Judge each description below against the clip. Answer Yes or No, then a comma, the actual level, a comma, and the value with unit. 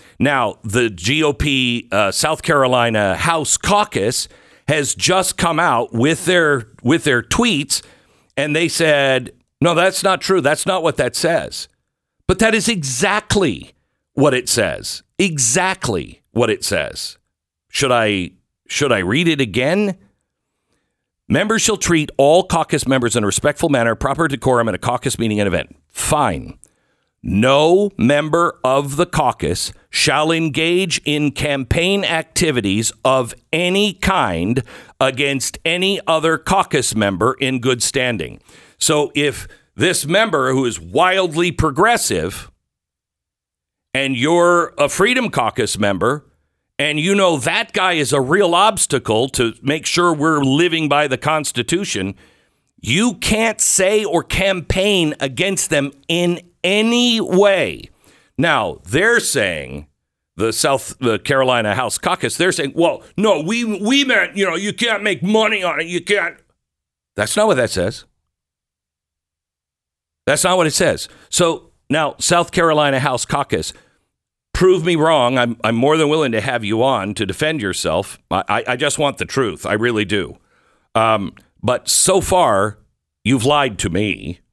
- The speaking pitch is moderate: Yes, medium, 150 Hz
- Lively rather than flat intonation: Yes, wide, 6.7 semitones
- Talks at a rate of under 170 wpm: Yes, average, 145 wpm